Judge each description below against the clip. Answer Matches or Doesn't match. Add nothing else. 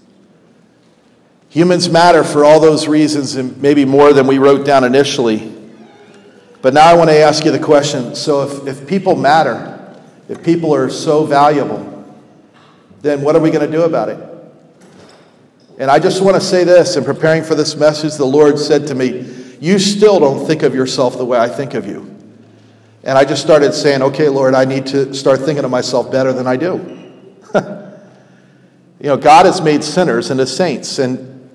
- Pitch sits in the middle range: Matches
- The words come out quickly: Doesn't match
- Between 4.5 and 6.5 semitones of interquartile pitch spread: Doesn't match